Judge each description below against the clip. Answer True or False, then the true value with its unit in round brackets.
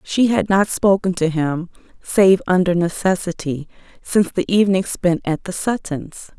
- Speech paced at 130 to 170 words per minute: True (150 wpm)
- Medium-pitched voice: True (180 Hz)